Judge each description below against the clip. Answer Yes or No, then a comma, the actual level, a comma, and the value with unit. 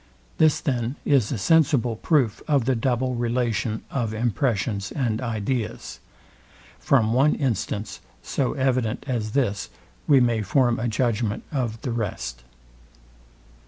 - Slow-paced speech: Yes, slow, 125 wpm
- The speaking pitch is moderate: No, low, 120 Hz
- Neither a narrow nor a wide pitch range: Yes, average, 3.3 semitones